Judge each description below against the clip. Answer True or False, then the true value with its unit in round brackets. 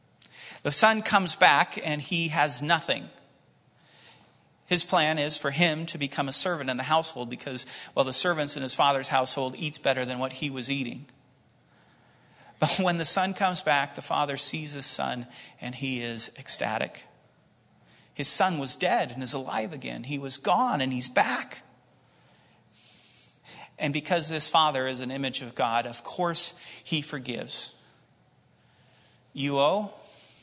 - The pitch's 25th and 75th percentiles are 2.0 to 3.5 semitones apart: False (4.3 semitones)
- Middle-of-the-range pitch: True (145 Hz)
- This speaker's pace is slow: False (155 wpm)